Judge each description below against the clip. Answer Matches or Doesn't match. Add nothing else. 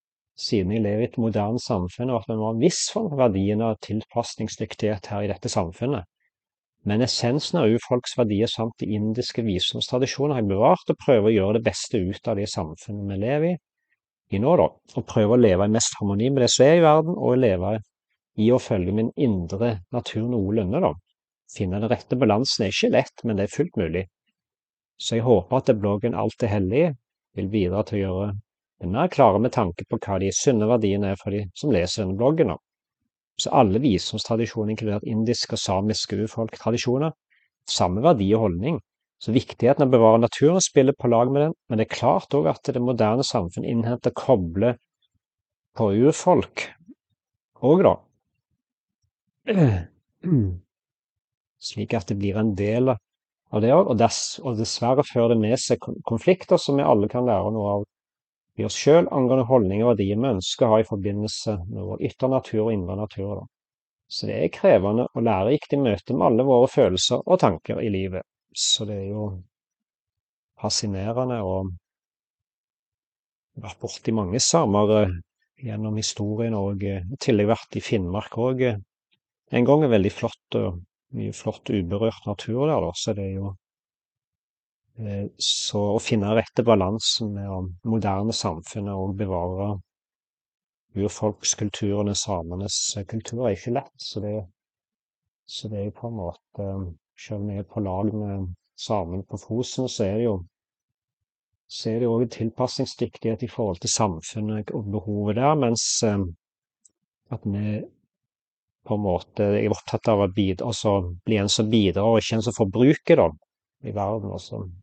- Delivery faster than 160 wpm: Matches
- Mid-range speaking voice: Doesn't match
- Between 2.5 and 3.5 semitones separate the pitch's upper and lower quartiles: Matches